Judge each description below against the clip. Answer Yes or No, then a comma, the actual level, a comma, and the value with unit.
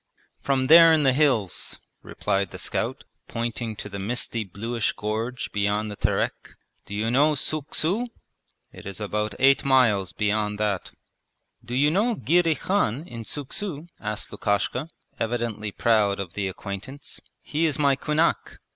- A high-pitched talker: No, low, 115 Hz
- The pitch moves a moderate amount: No, wide, 5.8 semitones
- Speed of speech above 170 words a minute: No, average, 155 wpm